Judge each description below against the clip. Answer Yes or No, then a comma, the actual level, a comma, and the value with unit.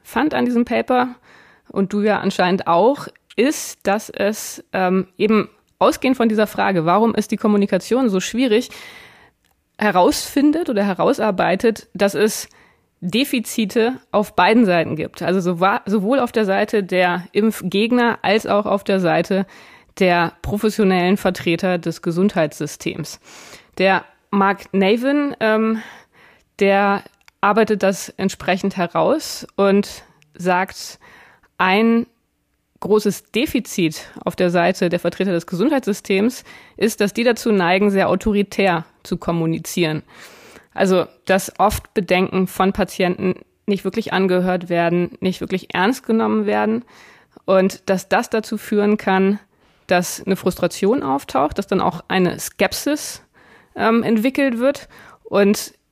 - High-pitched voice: Yes, high, 195 Hz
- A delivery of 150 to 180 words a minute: No, slow, 125 wpm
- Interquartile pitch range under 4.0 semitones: Yes, average, 3.3 semitones